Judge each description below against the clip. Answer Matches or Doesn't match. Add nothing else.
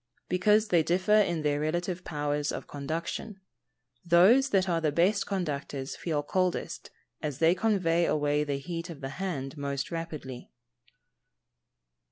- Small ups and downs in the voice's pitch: Doesn't match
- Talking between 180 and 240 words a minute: Doesn't match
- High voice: Doesn't match